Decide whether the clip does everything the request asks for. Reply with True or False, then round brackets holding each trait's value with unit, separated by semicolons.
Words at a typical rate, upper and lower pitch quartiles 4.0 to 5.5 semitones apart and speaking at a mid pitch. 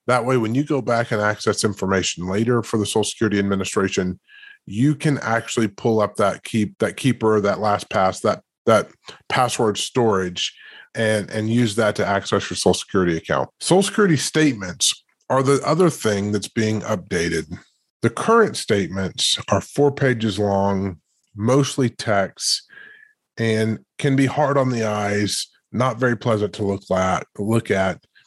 False (160 wpm; 4.6 semitones; 110 Hz)